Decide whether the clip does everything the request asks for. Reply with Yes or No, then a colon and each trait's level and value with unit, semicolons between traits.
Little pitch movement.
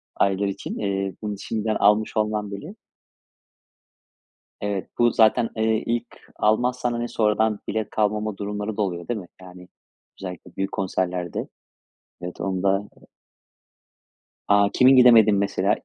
Yes: narrow, 2.2 semitones